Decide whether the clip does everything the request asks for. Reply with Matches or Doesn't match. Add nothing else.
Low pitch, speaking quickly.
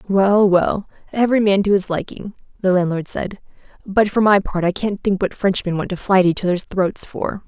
Doesn't match